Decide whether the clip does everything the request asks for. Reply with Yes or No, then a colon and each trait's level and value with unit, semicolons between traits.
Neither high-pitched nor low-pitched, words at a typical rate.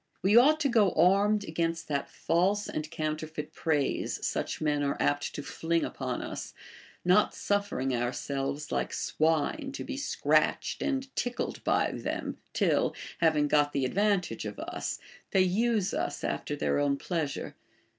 Yes: medium, 165 Hz; average, 155 wpm